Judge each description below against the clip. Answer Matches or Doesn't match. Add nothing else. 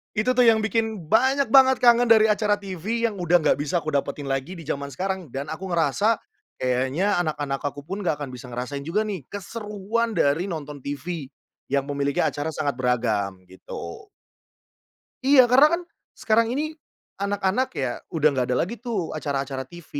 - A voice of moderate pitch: Matches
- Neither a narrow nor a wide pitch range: Doesn't match